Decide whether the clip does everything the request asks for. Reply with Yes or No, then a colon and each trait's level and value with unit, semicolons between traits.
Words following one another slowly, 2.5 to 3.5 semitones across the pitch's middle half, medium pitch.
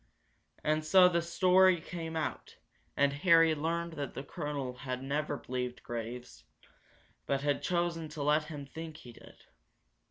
No: average, 150 wpm; average, 3.2 semitones; medium, 150 Hz